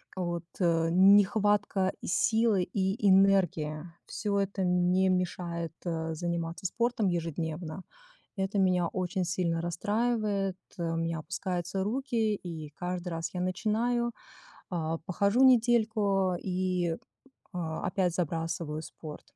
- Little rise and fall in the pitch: No, average, 3.1 semitones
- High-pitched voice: No, medium, 180 Hz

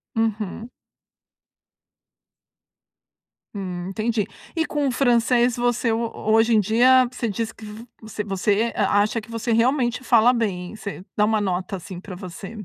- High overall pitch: Yes, high, 220 Hz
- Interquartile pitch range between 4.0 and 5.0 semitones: No, average, 2.7 semitones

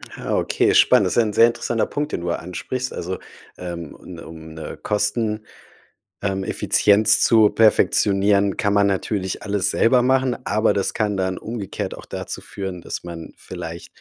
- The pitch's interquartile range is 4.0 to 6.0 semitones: No, average, 3.2 semitones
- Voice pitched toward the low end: Yes, low, 100 Hz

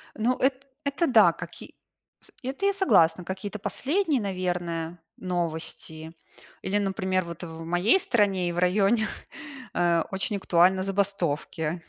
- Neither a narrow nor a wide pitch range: Yes, average, 4.0 semitones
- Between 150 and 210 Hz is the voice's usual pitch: Yes, high, 190 Hz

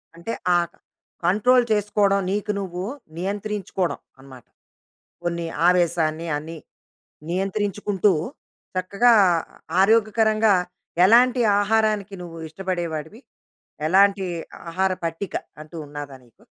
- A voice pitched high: Yes, high, 195 Hz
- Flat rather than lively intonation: No, average, 3.6 semitones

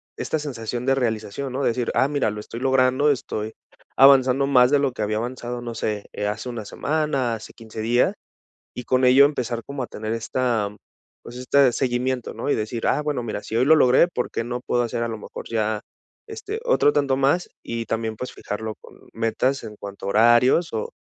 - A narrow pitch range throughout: No, average, 3.3 semitones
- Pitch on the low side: Yes, low, 125 Hz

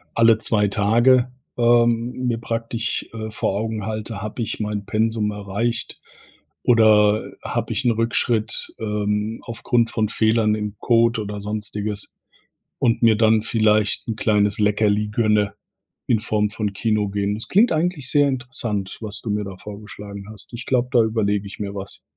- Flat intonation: Yes, narrow, 1.9 semitones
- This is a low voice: Yes, low, 110 Hz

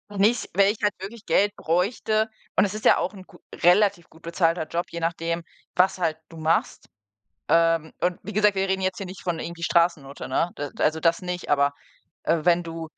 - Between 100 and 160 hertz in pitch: No, medium, 175 Hz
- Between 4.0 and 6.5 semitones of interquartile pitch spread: No, average, 2.7 semitones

